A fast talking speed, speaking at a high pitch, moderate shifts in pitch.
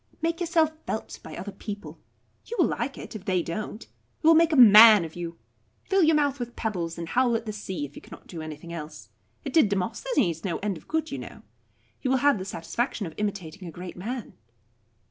No: fast, 220 wpm; high, 210 Hz; wide, 7.4 semitones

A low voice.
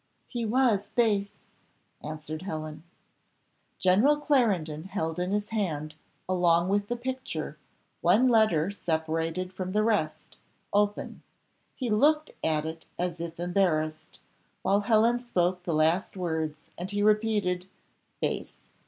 No: medium, 185 Hz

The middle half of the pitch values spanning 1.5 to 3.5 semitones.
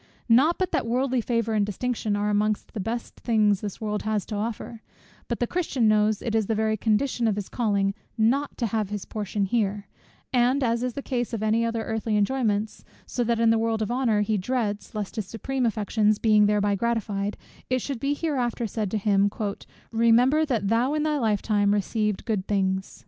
Yes: narrow, 2.5 semitones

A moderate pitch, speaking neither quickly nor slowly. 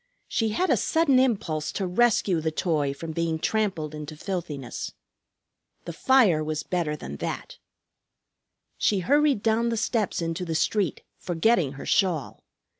Yes: medium, 175 Hz; average, 145 wpm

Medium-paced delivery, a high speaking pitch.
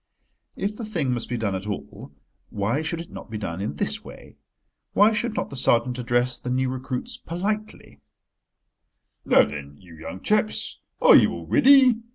No: average, 180 wpm; low, 130 Hz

